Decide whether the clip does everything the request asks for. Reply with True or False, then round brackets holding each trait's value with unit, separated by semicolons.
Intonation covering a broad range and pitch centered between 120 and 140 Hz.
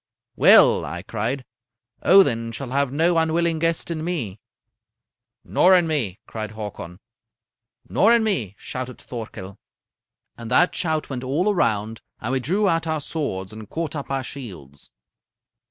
True (7.1 semitones; 135 Hz)